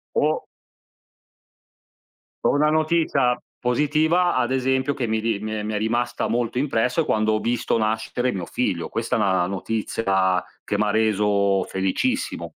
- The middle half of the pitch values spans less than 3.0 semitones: No, average, 3.9 semitones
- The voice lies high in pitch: No, low, 115 Hz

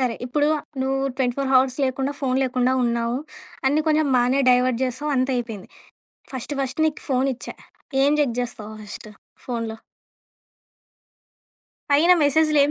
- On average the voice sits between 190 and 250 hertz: No, very high, 260 Hz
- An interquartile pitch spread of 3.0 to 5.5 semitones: No, narrow, 2.6 semitones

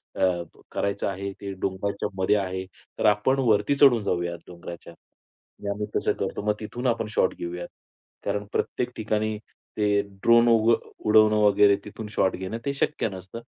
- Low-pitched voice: Yes, low, 105 Hz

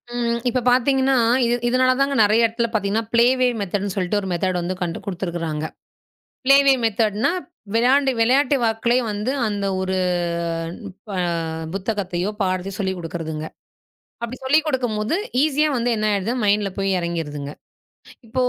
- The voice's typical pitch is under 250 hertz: Yes, high, 215 Hz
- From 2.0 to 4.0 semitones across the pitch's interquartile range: No, average, 4.8 semitones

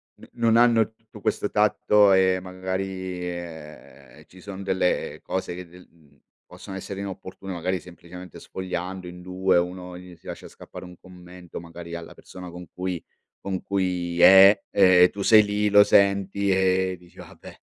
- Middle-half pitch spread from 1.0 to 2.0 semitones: Yes, narrow, 1.6 semitones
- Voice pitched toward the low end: Yes, very low, 95 Hz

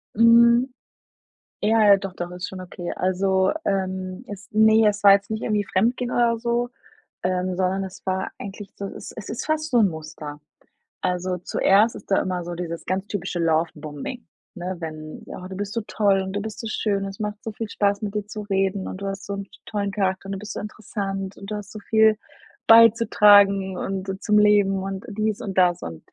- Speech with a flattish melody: Yes, narrow, 2.3 semitones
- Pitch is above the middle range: Yes, high, 195 Hz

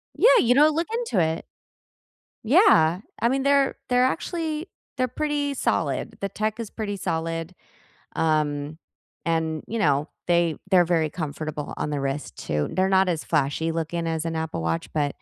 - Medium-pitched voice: Yes, medium, 170 Hz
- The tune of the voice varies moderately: No, wide, 8.1 semitones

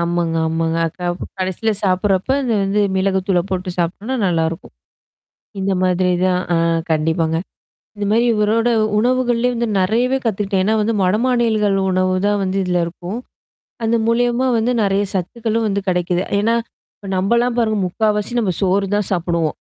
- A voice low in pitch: No, high, 195 Hz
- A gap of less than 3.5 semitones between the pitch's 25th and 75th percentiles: No, average, 3.8 semitones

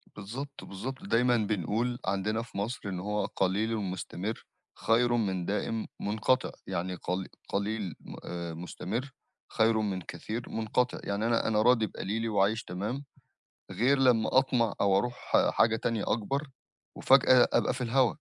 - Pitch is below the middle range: Yes, low, 110 Hz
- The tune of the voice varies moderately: Yes, average, 3.7 semitones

